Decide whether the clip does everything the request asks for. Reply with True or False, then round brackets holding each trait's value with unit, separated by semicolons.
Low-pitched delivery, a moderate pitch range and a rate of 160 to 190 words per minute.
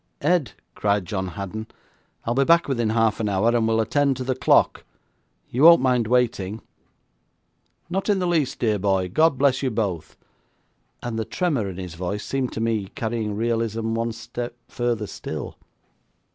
True (115 Hz; 3.7 semitones; 170 wpm)